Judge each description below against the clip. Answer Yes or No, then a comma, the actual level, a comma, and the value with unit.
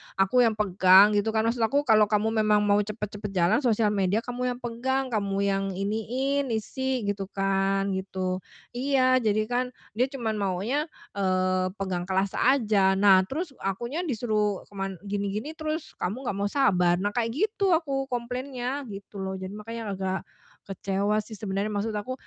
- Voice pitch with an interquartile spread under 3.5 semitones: No, average, 4.3 semitones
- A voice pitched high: Yes, high, 210 Hz